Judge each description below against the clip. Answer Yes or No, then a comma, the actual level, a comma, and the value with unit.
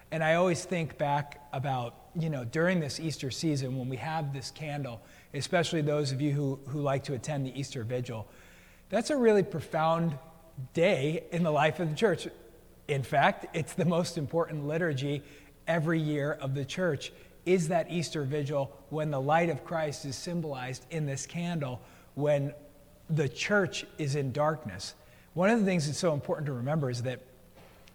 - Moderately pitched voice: Yes, medium, 150 Hz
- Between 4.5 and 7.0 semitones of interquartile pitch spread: No, average, 3.3 semitones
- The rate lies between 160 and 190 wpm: Yes, average, 180 wpm